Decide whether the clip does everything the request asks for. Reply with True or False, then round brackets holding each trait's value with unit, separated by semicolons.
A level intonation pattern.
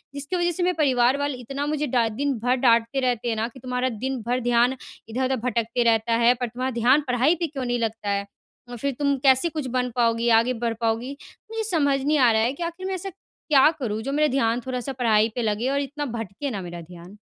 False (3.4 semitones)